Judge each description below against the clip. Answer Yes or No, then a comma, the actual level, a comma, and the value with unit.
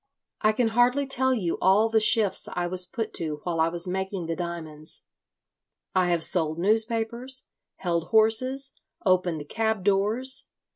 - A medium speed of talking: Yes, average, 150 wpm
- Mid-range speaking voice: No, high, 195 Hz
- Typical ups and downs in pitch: Yes, average, 4.6 semitones